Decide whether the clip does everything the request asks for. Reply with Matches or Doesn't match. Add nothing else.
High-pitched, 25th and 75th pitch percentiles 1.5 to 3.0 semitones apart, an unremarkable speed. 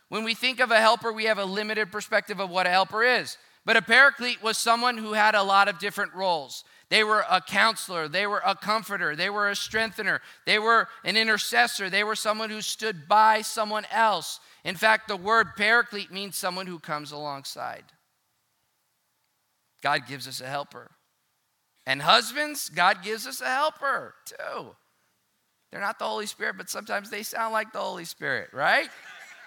Matches